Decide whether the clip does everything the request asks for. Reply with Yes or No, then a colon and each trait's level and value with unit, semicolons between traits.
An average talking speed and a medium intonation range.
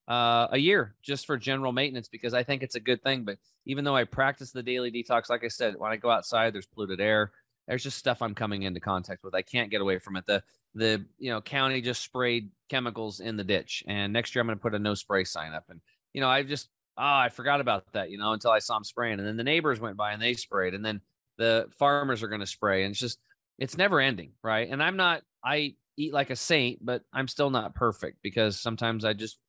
No: fast, 255 wpm; average, 3.5 semitones